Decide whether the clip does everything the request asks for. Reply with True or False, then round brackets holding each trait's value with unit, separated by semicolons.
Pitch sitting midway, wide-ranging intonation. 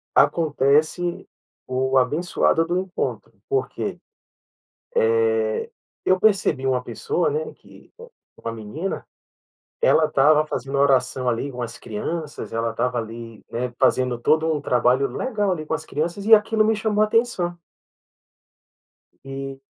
True (155 Hz; 8.3 semitones)